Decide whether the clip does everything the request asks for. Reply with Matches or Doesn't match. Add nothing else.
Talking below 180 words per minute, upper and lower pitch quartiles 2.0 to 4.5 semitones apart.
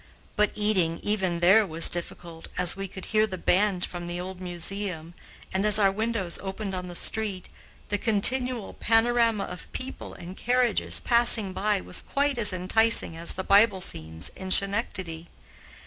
Matches